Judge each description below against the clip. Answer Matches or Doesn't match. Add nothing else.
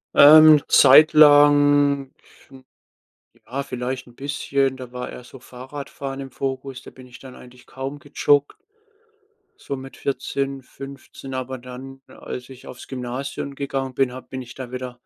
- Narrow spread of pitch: Matches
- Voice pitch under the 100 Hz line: Doesn't match